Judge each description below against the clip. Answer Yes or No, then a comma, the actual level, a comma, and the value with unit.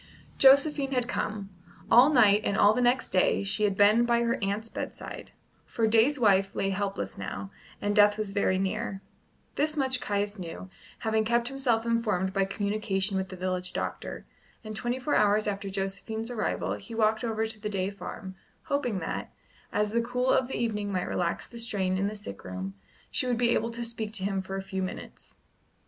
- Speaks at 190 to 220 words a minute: Yes, average, 195 wpm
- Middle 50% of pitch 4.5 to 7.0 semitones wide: No, average, 3.2 semitones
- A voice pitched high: Yes, high, 210 Hz